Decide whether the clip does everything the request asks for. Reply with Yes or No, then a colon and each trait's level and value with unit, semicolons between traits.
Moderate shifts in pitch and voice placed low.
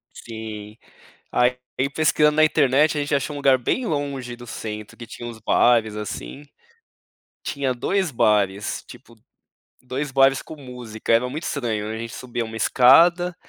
Yes: average, 4.3 semitones; low, 125 Hz